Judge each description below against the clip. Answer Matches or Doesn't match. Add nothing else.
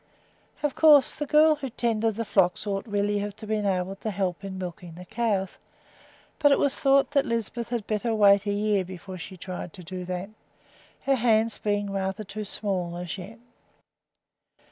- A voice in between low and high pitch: Doesn't match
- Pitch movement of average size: Matches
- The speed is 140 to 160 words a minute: Doesn't match